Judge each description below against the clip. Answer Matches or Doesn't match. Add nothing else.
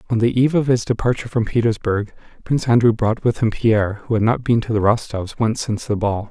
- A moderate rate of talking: Doesn't match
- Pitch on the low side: Matches